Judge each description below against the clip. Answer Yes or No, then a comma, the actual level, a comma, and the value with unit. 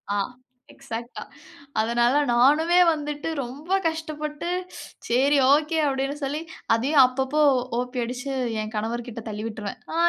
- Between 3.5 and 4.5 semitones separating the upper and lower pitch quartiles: Yes, average, 3.9 semitones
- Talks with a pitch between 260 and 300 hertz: Yes, very high, 270 Hz